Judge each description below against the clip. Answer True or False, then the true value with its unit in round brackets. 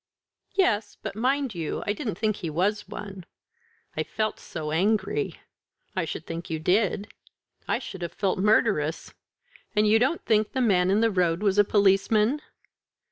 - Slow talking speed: False (165 wpm)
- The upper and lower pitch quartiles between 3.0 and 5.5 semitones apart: True (3.3 semitones)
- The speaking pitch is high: True (205 Hz)